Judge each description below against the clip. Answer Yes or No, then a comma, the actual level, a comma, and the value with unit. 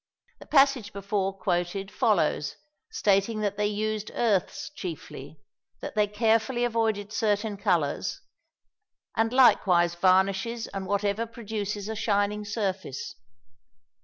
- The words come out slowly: Yes, slow, 110 wpm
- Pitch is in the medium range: No, high, 205 Hz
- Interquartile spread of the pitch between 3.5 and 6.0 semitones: No, narrow, 2.4 semitones